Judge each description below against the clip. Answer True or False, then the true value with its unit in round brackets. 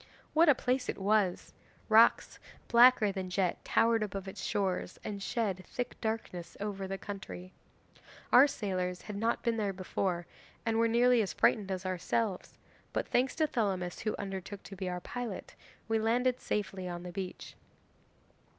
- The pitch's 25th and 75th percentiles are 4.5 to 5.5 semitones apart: False (3.5 semitones)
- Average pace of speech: True (160 wpm)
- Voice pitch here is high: True (205 Hz)